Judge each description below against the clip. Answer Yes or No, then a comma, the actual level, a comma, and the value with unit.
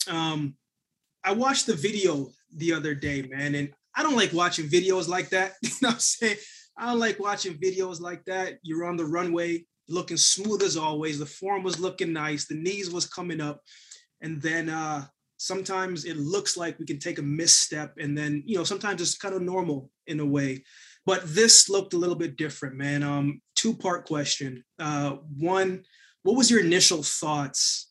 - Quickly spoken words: No, average, 195 wpm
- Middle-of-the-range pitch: Yes, medium, 170 Hz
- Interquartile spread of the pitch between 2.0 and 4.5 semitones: Yes, average, 3.9 semitones